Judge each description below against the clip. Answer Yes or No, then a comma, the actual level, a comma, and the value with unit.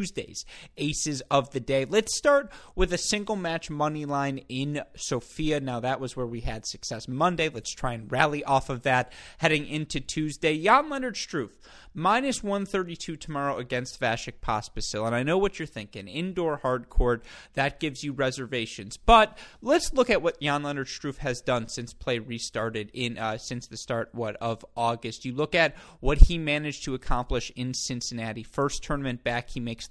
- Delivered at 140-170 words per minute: No, average, 185 wpm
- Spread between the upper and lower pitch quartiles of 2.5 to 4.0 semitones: No, average, 4.6 semitones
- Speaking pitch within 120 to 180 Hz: Yes, low, 135 Hz